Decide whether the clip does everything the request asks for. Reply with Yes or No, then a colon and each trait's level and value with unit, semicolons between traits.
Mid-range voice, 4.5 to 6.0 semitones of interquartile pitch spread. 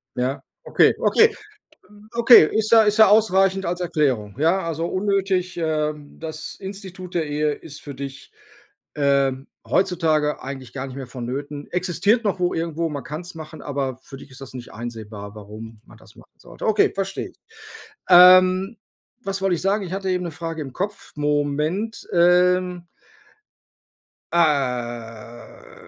Yes: medium, 160 Hz; average, 5.2 semitones